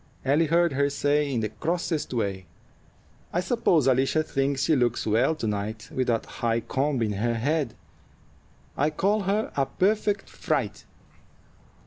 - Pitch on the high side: No, medium, 140 Hz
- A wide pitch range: Yes, wide, 5.7 semitones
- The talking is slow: No, average, 150 wpm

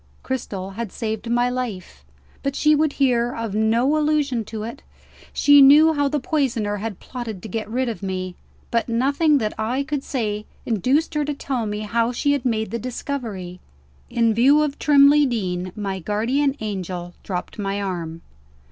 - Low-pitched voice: No, high, 235 Hz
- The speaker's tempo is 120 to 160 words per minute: No, average, 175 wpm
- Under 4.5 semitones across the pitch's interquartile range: No, average, 5.0 semitones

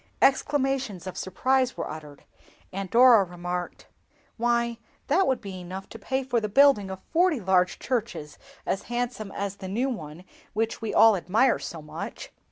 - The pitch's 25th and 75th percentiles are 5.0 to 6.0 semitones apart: Yes, wide, 5.4 semitones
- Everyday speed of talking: Yes, average, 160 wpm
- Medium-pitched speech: No, high, 215 Hz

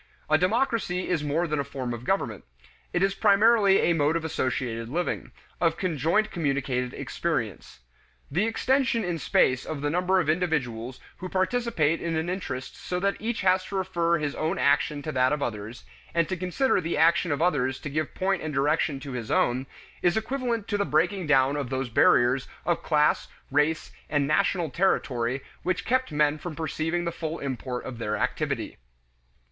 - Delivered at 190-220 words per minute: No, average, 180 wpm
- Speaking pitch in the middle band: Yes, medium, 160 Hz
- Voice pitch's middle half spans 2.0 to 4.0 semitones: No, average, 5.0 semitones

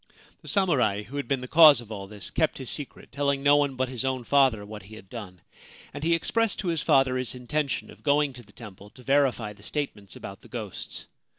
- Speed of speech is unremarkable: No, fast, 230 wpm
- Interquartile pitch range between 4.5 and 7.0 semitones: Yes, average, 5.0 semitones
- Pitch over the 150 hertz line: No, low, 130 Hz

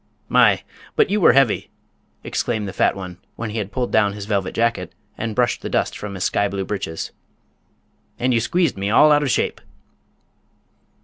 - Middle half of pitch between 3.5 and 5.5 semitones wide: Yes, average, 3.8 semitones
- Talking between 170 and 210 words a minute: Yes, average, 185 wpm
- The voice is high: No, low, 105 Hz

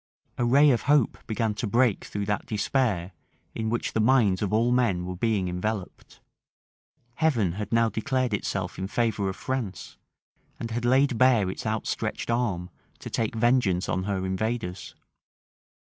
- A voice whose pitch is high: No, low, 110 Hz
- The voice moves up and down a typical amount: Yes, average, 3.9 semitones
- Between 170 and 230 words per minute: No, average, 160 wpm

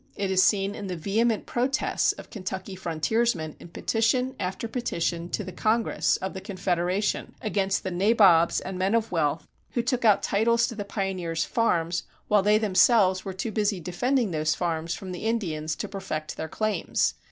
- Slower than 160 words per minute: No, average, 175 wpm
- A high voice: Yes, high, 195 Hz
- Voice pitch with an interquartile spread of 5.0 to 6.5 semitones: No, average, 4.0 semitones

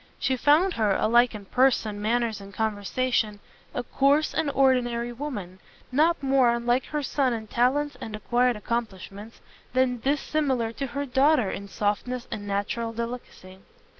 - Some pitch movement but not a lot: Yes, average, 3.9 semitones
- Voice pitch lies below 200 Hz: No, high, 240 Hz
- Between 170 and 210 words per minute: No, average, 145 wpm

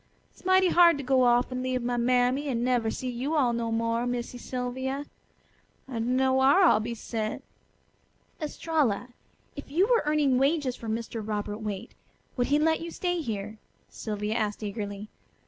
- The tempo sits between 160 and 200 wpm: Yes, average, 170 wpm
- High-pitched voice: Yes, very high, 250 Hz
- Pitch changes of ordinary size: Yes, average, 3.9 semitones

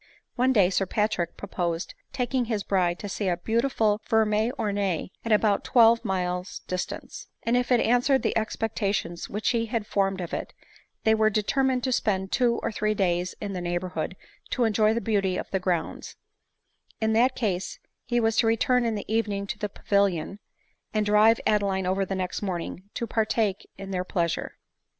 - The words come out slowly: No, average, 180 wpm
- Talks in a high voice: Yes, high, 210 Hz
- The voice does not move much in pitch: No, average, 3.2 semitones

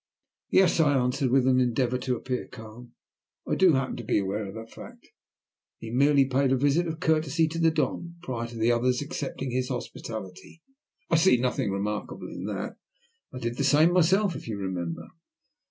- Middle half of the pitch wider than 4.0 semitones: Yes, average, 4.8 semitones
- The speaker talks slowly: No, average, 185 wpm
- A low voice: Yes, low, 130 Hz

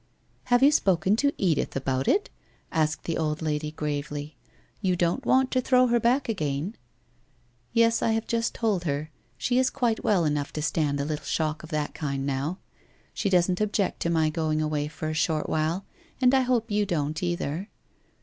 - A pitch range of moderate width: No, wide, 6.7 semitones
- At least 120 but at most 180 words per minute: No, average, 200 wpm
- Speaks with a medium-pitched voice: Yes, medium, 165 Hz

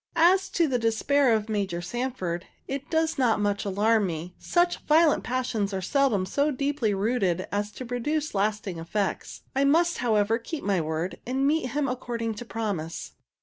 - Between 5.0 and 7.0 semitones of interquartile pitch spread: Yes, wide, 5.6 semitones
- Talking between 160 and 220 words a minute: Yes, average, 170 wpm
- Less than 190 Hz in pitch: No, high, 230 Hz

